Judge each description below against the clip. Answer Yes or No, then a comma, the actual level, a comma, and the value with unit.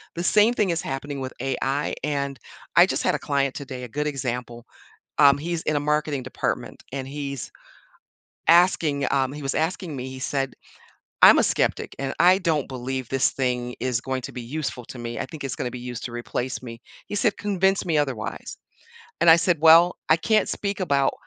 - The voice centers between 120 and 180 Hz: Yes, medium, 140 Hz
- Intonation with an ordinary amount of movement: Yes, average, 4.0 semitones